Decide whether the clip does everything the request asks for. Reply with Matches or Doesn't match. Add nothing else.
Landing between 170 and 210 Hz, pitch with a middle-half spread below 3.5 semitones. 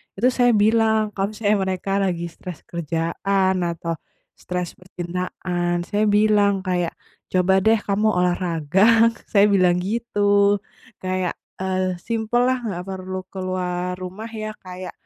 Matches